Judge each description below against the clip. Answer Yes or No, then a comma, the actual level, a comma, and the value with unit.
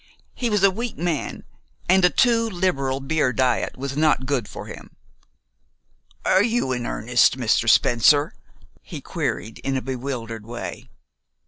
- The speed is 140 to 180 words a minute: Yes, average, 145 wpm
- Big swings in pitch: Yes, wide, 6.9 semitones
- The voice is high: No, low, 135 Hz